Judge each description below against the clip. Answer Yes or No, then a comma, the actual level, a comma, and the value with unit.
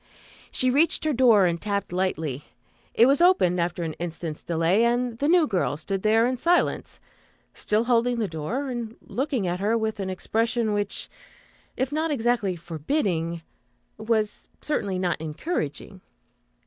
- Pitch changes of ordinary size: No, wide, 5.9 semitones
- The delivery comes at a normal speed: Yes, average, 150 wpm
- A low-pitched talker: No, high, 215 Hz